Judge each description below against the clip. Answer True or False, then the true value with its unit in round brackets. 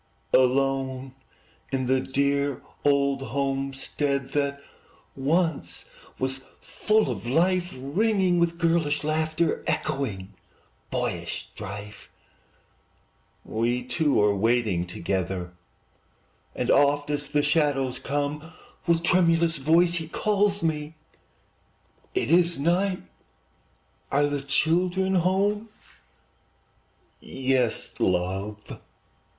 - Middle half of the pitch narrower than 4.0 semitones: False (4.4 semitones)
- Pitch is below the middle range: False (145 Hz)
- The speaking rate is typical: False (90 wpm)